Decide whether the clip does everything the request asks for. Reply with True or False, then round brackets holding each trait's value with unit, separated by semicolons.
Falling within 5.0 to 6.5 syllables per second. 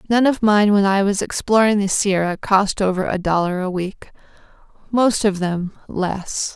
False (4.4 syllables/s)